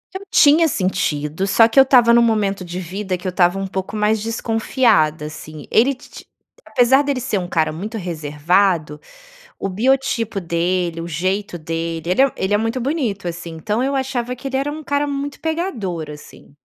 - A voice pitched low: No, high, 200 Hz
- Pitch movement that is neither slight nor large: No, wide, 6.7 semitones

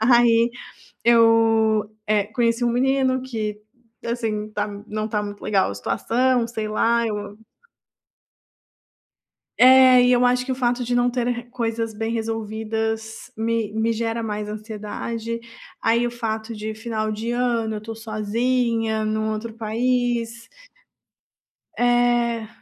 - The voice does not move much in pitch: Yes, narrow, 1.8 semitones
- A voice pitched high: Yes, high, 225 Hz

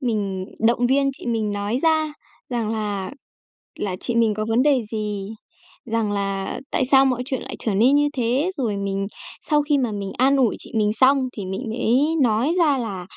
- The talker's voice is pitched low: No, high, 230 Hz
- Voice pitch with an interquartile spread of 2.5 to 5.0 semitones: Yes, average, 4.5 semitones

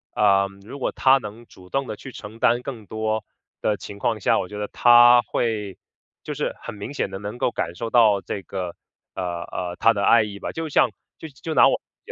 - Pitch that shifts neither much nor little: Yes, average, 3.4 semitones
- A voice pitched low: Yes, low, 105 Hz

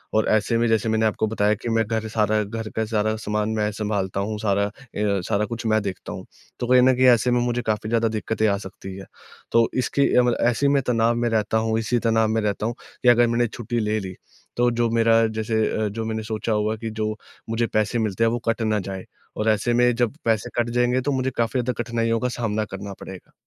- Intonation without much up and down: Yes, narrow, 1.7 semitones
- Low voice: Yes, low, 110 Hz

